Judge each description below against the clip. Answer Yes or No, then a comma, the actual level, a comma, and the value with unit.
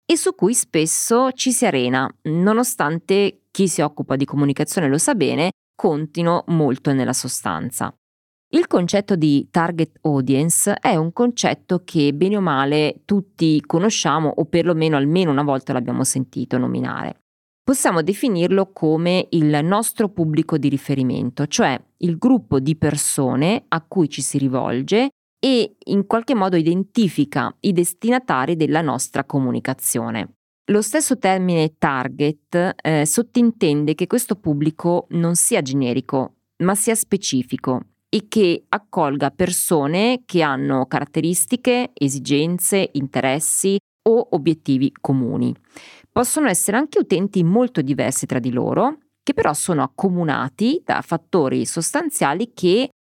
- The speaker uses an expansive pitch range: Yes, wide, 6.1 semitones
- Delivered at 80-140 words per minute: Yes, average, 130 wpm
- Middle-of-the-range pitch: Yes, medium, 165 Hz